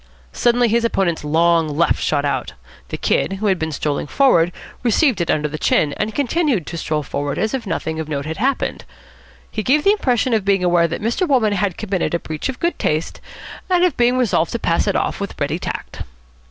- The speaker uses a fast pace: Yes, fast, 215 wpm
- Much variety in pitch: Yes, wide, 7.1 semitones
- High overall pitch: Yes, high, 195 Hz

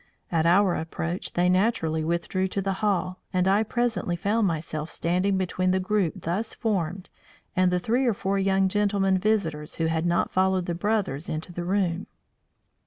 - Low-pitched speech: No, medium, 185 Hz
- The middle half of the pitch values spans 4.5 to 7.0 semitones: No, narrow, 2.6 semitones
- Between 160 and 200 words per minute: Yes, average, 175 wpm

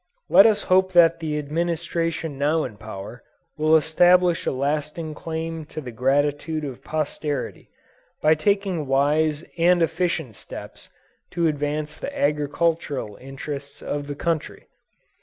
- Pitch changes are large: No, average, 2.7 semitones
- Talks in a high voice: No, medium, 155 Hz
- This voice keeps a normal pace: No, slow, 130 wpm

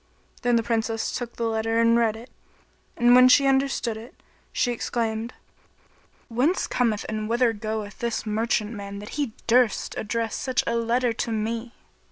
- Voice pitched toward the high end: Yes, high, 230 Hz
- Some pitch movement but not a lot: No, narrow, 1.7 semitones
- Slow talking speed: No, average, 165 wpm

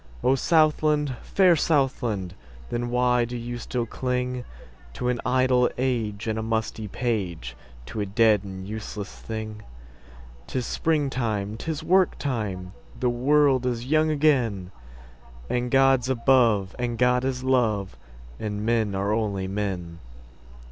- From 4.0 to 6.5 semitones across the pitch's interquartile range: Yes, average, 4.7 semitones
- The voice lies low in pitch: Yes, low, 115 Hz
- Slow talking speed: Yes, slow, 115 wpm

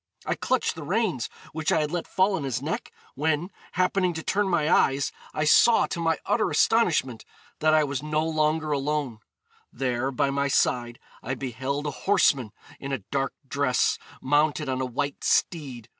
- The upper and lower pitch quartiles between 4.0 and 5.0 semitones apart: No, average, 3.3 semitones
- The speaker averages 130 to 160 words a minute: No, average, 175 wpm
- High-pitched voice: No, medium, 150 Hz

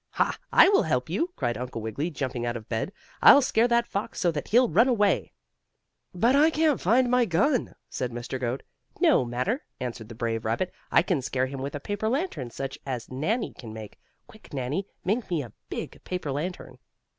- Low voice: No, medium, 155 Hz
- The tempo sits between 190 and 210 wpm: Yes, average, 200 wpm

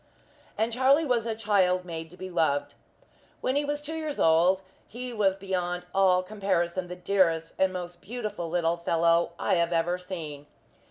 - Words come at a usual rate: Yes, average, 170 wpm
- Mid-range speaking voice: Yes, medium, 180 Hz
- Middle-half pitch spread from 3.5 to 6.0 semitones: Yes, average, 3.9 semitones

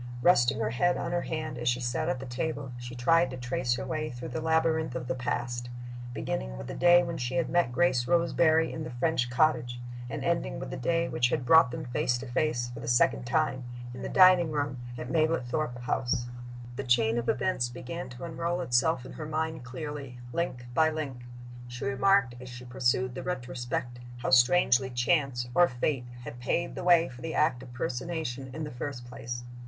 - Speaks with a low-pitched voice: Yes, low, 130 Hz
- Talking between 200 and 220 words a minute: Yes, fast, 205 wpm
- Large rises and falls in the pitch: No, average, 4.6 semitones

